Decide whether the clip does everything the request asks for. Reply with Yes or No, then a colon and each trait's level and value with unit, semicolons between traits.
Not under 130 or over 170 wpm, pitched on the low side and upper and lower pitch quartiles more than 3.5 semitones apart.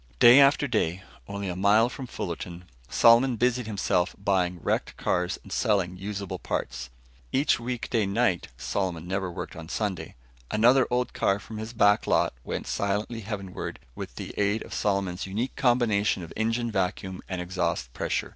Yes: average, 160 wpm; low, 100 Hz; average, 4.1 semitones